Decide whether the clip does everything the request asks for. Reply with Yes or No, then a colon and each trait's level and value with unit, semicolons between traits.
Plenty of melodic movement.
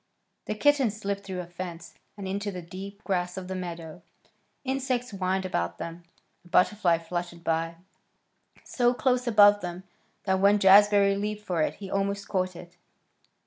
No: average, 2.7 semitones